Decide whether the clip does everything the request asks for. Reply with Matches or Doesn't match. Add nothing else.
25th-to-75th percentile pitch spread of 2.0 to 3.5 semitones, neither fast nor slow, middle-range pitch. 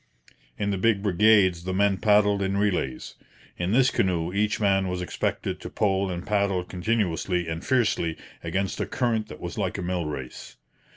Doesn't match